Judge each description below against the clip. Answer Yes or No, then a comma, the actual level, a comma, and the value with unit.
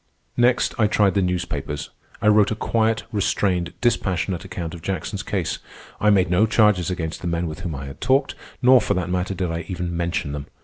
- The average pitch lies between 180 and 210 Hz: No, very low, 90 Hz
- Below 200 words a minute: No, fast, 205 wpm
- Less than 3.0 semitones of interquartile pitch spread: No, average, 3.6 semitones